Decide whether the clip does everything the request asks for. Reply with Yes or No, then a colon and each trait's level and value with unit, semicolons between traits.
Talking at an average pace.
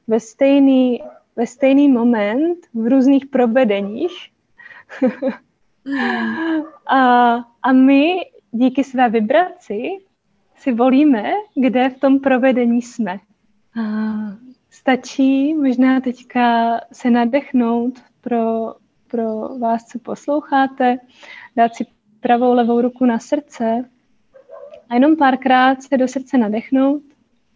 No: slow, 100 wpm